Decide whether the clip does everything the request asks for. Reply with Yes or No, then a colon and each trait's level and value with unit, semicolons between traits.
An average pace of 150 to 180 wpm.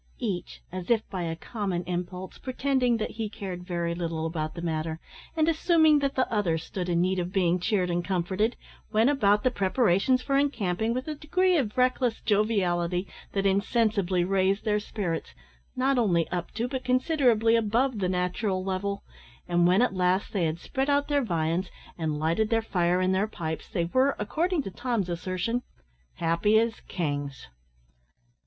Yes: average, 175 wpm